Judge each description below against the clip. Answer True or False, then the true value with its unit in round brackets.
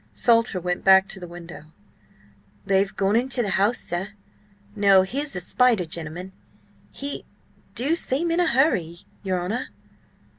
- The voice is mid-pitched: False (195 Hz)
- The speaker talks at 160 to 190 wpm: False (145 wpm)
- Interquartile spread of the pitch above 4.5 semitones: True (5.6 semitones)